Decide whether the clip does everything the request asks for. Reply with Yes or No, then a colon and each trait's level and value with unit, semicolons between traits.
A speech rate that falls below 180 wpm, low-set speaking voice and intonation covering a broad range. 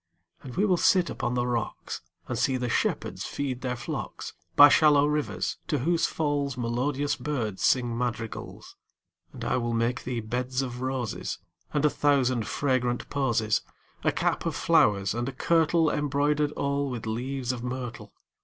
No: average, 170 wpm; low, 130 Hz; average, 3.2 semitones